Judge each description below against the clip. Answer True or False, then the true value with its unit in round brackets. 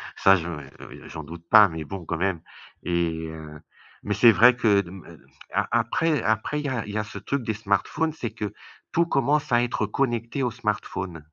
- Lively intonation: True (5.9 semitones)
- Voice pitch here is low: True (105 Hz)